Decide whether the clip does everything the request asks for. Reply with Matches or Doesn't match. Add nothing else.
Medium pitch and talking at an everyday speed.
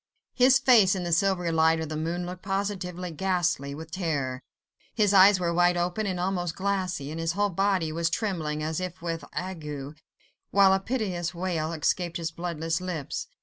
Matches